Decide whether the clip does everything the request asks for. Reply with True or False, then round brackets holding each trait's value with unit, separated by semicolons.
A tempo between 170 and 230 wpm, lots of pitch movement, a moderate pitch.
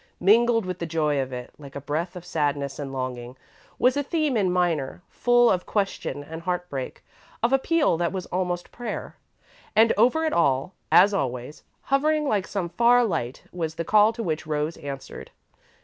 True (180 wpm; 7.6 semitones; 175 Hz)